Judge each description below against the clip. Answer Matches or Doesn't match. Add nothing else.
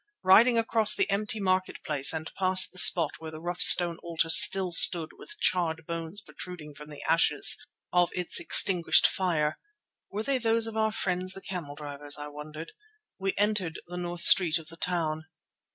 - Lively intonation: Doesn't match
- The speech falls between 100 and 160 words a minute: Doesn't match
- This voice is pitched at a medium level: Matches